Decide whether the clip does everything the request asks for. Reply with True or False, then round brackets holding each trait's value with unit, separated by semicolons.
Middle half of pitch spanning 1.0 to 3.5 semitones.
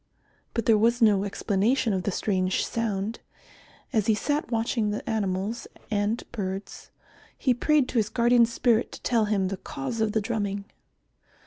True (2.8 semitones)